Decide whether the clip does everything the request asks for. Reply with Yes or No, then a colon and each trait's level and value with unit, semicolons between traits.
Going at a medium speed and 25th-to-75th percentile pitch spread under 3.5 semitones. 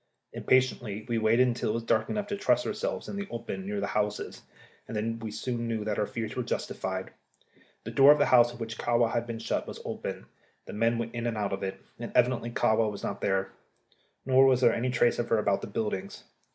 No: fast, 230 wpm; narrow, 2.4 semitones